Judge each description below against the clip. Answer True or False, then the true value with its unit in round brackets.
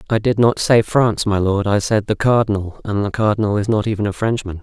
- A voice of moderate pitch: False (105 Hz)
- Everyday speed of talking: False (245 wpm)